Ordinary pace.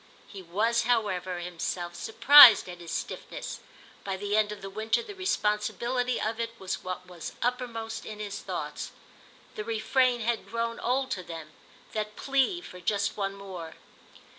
Yes: average, 160 wpm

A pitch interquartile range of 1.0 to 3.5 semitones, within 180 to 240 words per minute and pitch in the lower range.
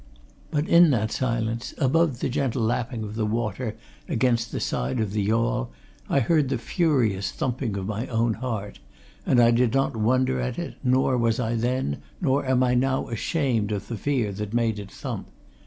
Yes: average, 3.0 semitones; average, 190 wpm; low, 120 Hz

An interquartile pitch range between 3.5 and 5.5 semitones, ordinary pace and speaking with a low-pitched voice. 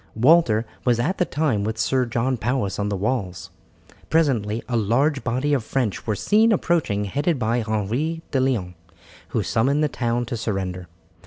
Yes: average, 4.9 semitones; average, 170 wpm; low, 120 Hz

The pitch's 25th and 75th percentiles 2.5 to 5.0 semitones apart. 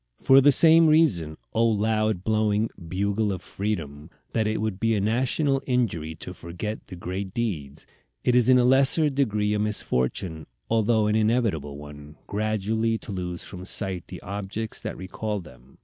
Yes: average, 4.1 semitones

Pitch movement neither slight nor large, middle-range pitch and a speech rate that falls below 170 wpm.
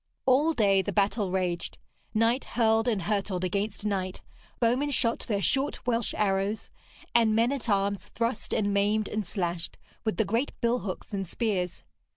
No: average, 3.0 semitones; high, 210 Hz; average, 160 wpm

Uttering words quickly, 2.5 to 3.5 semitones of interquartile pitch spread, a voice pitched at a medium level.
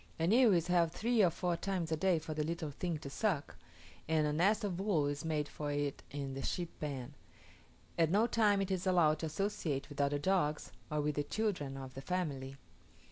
No: fast, 215 wpm; average, 4.4 semitones; medium, 160 Hz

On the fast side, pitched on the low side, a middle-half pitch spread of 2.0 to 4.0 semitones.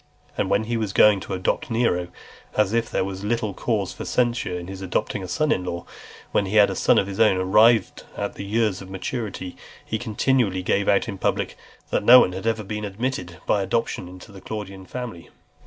Yes: fast, 210 wpm; low, 100 Hz; average, 3.2 semitones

